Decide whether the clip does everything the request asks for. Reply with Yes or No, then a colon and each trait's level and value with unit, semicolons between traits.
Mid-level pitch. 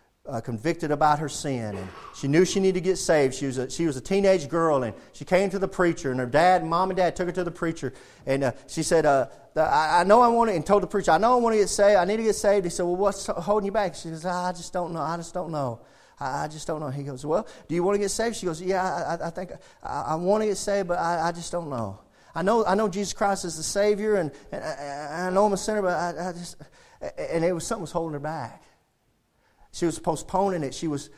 Yes: medium, 175 Hz